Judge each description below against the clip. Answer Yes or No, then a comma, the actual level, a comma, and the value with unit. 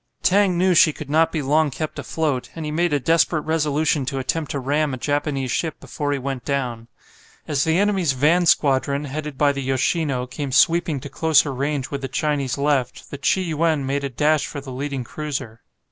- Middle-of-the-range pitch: Yes, medium, 145 Hz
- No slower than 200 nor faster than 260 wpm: Yes, fast, 205 wpm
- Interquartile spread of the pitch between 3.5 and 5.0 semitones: No, average, 2.7 semitones